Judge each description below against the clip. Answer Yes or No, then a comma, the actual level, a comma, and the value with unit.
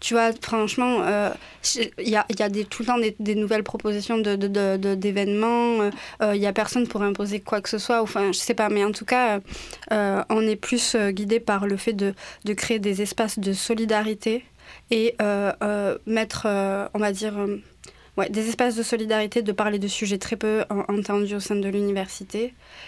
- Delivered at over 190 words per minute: Yes, fast, 220 wpm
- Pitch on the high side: Yes, high, 210 Hz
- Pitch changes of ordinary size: No, narrow, 1.9 semitones